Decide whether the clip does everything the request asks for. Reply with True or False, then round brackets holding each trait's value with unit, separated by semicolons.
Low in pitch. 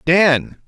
False (165 Hz)